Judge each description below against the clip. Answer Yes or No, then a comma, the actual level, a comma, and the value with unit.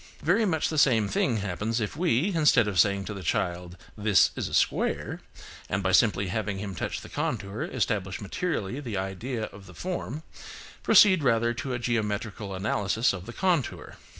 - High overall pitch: No, low, 110 Hz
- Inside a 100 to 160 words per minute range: No, average, 180 wpm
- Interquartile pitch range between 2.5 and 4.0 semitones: No, wide, 5.4 semitones